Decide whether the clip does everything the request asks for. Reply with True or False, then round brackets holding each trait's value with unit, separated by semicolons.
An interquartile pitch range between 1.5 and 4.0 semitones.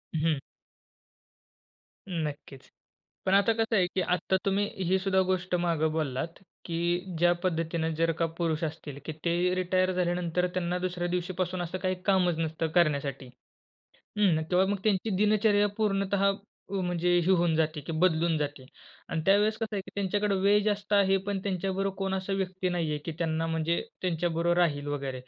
True (2.8 semitones)